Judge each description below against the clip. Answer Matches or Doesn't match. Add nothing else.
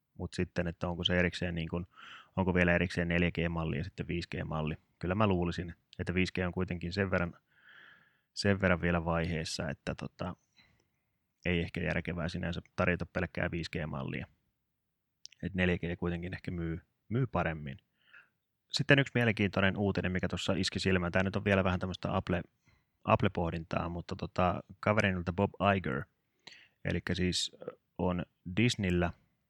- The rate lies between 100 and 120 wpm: Doesn't match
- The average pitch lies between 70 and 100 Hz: Matches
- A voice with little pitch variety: Matches